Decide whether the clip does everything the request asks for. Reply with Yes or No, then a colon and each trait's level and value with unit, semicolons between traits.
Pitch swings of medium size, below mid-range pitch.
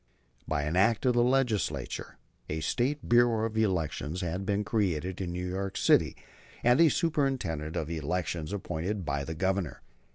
No: wide, 6.0 semitones; very low, 95 Hz